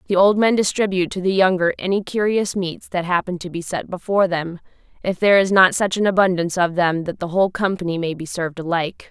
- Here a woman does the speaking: Yes, female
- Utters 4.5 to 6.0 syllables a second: No, 6.2 syllables/s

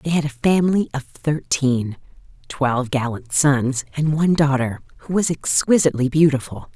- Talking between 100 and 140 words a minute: Yes, slow, 135 wpm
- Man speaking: No, female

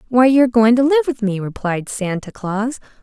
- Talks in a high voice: Yes, high, 225 Hz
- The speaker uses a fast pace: Yes, fast, 220 wpm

